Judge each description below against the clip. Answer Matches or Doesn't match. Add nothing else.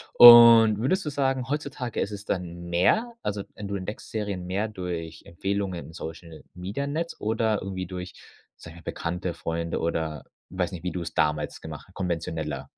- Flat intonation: Doesn't match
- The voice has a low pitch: Matches